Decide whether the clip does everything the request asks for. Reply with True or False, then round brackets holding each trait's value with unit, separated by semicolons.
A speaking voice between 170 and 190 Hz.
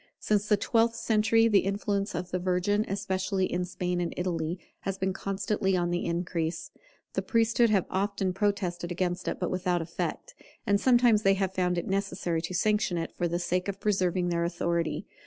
True (185 Hz)